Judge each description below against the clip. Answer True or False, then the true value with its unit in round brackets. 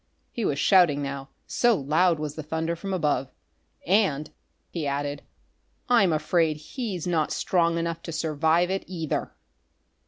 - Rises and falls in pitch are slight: False (3.2 semitones)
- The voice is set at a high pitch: False (160 Hz)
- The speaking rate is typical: True (145 wpm)